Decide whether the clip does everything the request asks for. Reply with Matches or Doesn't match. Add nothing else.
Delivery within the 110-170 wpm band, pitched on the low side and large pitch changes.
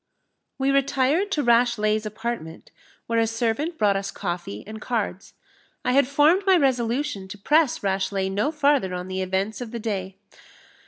Doesn't match